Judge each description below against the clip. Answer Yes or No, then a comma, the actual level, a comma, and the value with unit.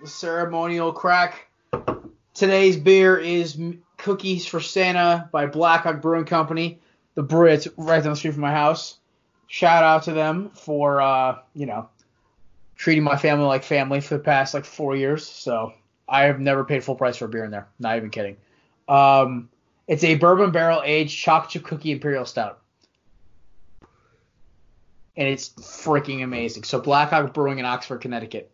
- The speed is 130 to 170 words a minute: Yes, average, 160 wpm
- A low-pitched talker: No, medium, 150 Hz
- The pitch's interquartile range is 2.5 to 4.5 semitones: Yes, average, 3.5 semitones